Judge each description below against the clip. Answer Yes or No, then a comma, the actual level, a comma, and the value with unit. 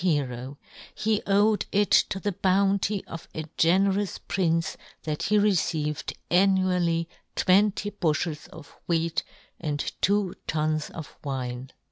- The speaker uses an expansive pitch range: No, average, 4.3 semitones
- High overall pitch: No, medium, 175 Hz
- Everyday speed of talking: No, slow, 120 wpm